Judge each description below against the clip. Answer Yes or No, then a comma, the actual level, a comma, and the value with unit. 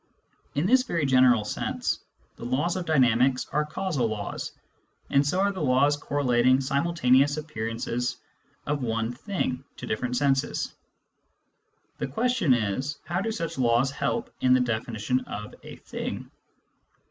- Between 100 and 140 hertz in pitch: Yes, low, 135 Hz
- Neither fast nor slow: Yes, average, 155 wpm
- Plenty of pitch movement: No, average, 4.1 semitones